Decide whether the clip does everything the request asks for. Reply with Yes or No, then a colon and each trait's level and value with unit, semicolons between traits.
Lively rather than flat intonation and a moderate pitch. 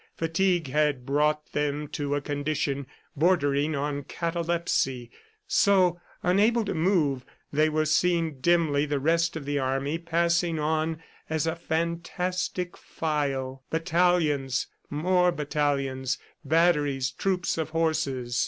No: average, 3.2 semitones; medium, 155 Hz